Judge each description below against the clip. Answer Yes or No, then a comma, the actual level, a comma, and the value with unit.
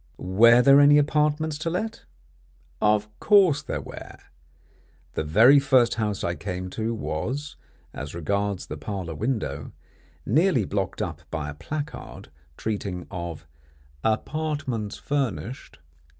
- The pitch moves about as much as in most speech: No, wide, 7.8 semitones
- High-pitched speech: No, low, 110 Hz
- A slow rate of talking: Yes, slow, 120 wpm